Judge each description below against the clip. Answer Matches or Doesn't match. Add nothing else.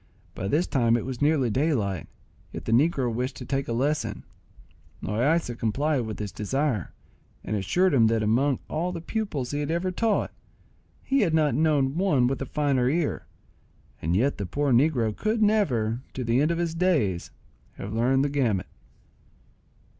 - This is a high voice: Doesn't match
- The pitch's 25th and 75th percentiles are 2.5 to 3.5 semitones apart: Doesn't match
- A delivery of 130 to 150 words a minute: Doesn't match